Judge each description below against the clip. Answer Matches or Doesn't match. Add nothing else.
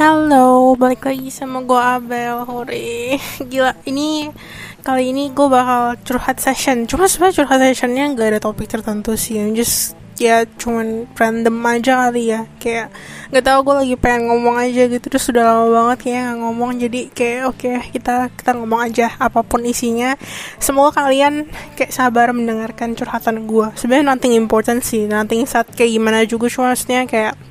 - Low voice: Doesn't match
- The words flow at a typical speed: Doesn't match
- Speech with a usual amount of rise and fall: Doesn't match